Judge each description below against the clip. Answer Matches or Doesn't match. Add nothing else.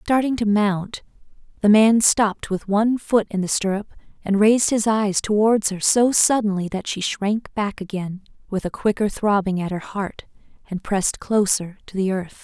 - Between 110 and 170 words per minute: Doesn't match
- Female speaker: Matches